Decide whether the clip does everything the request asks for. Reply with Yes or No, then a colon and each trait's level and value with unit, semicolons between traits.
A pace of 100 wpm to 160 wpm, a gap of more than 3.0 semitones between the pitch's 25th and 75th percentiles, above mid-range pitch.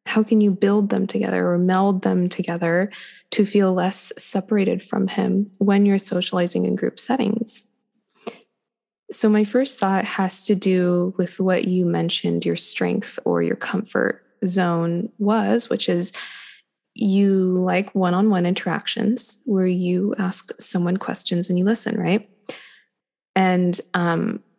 Yes: average, 145 wpm; average, 3.4 semitones; high, 200 Hz